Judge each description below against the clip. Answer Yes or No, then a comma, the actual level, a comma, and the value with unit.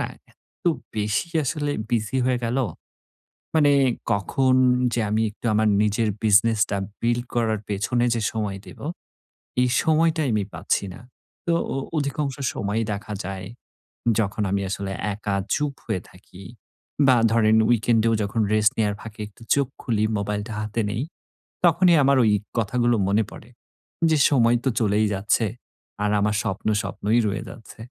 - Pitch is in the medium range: No, low, 110 Hz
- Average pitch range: Yes, average, 3.1 semitones